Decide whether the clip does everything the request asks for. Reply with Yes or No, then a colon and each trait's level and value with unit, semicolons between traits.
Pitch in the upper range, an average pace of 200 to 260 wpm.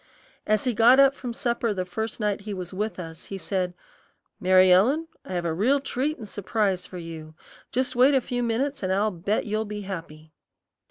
Yes: high, 210 Hz; fast, 205 wpm